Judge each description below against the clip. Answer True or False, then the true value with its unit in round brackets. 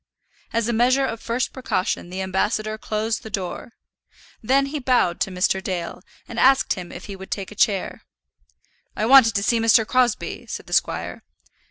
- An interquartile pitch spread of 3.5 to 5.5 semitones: True (4.2 semitones)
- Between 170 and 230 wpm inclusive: True (180 wpm)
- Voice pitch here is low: False (220 Hz)